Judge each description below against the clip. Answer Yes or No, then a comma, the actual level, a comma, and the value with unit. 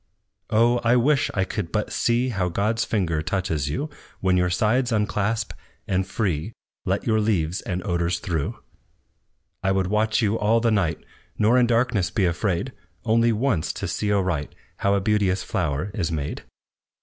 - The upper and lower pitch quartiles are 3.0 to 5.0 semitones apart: Yes, average, 4.0 semitones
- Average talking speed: Yes, average, 165 wpm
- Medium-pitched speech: No, low, 100 Hz